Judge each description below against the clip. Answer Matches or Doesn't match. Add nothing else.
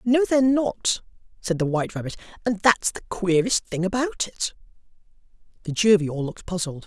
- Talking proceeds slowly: Doesn't match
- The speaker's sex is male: Matches